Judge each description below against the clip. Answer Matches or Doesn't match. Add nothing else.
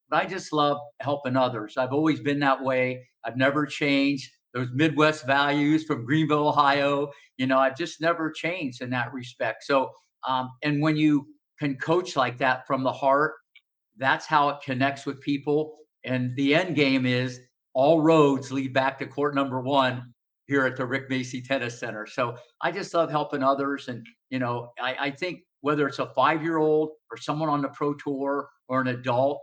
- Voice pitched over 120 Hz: Matches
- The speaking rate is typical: Matches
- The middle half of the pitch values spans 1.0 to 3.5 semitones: Matches